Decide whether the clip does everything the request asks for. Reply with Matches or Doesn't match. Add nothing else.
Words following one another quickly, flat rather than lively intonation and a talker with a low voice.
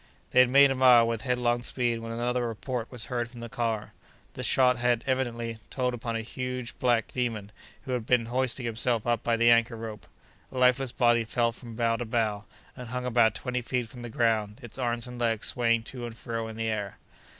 Matches